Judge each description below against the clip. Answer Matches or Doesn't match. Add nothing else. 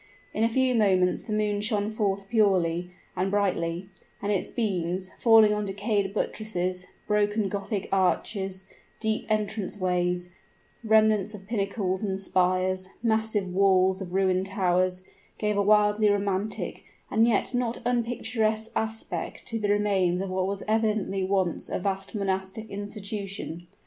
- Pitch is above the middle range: Matches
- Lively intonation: Doesn't match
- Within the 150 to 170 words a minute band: Doesn't match